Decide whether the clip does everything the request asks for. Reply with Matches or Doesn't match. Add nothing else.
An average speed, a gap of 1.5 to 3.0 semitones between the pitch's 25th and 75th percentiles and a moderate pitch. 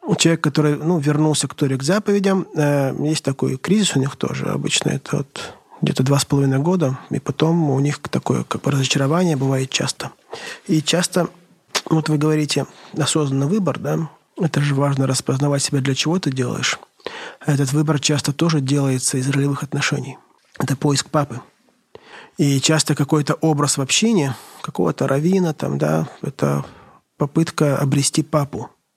Matches